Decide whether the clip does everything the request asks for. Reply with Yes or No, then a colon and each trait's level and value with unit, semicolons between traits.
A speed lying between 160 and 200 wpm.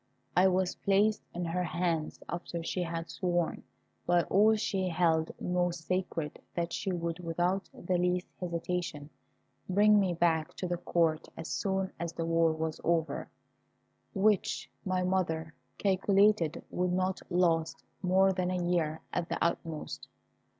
No: average, 145 wpm